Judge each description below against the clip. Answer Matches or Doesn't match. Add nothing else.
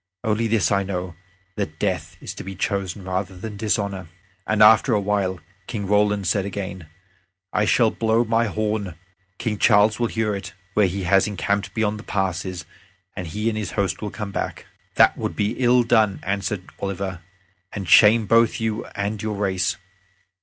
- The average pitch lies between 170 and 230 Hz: Doesn't match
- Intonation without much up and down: Matches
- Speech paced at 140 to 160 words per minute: Doesn't match